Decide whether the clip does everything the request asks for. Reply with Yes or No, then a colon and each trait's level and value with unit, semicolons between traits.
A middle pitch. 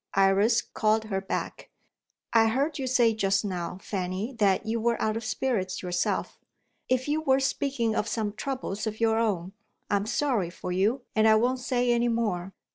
No: high, 220 Hz